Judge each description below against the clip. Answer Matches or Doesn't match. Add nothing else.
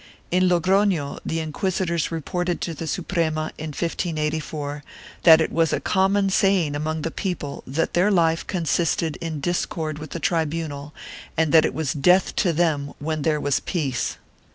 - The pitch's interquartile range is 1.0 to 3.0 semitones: Matches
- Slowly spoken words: Doesn't match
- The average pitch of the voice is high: Doesn't match